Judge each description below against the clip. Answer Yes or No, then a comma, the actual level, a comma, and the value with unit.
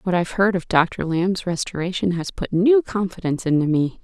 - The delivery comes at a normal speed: No, fast, 210 wpm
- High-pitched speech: No, medium, 180 Hz